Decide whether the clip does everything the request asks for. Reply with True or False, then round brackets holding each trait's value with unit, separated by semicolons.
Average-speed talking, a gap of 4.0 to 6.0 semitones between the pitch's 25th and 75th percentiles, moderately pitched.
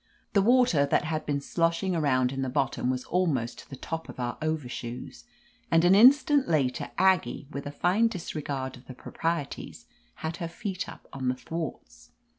True (180 wpm; 5.2 semitones; 155 Hz)